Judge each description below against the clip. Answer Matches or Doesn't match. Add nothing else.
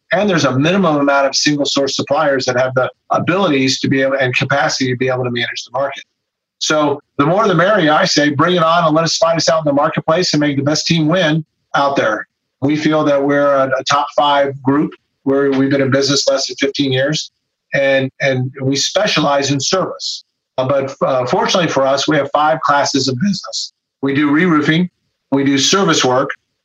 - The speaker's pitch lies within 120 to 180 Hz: Matches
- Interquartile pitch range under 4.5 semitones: Matches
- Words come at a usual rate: Doesn't match